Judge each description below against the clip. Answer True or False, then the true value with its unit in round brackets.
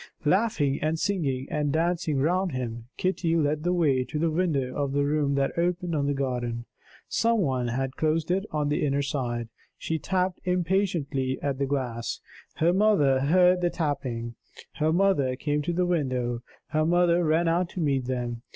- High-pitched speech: False (150 Hz)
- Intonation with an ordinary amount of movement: True (4.7 semitones)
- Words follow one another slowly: False (180 wpm)